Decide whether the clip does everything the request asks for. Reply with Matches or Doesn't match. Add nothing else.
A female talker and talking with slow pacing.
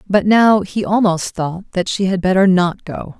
Doesn't match